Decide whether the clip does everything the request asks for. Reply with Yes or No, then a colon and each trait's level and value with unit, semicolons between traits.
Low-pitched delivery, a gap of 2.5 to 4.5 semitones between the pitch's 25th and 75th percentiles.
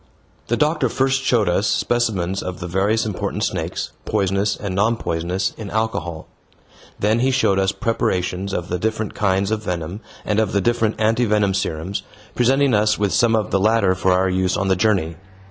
Yes: low, 100 Hz; average, 3.2 semitones